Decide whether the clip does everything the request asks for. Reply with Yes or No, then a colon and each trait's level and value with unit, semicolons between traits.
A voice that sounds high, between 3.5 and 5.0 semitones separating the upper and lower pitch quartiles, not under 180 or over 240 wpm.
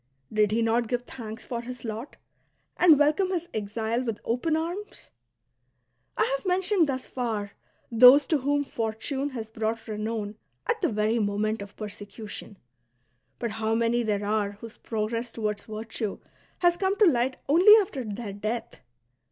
No: high, 230 Hz; average, 4.5 semitones; average, 155 wpm